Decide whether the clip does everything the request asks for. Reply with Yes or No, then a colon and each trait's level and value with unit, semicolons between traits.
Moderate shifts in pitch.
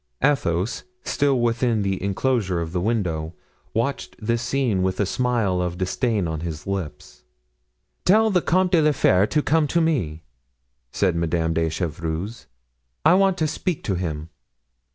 No: wide, 8.1 semitones